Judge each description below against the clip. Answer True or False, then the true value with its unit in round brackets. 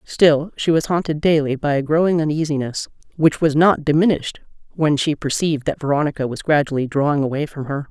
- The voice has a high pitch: False (150 Hz)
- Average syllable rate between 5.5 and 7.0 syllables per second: True (5.9 syllables/s)